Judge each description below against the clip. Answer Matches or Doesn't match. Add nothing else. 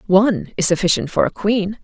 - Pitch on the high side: Matches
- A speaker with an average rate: Matches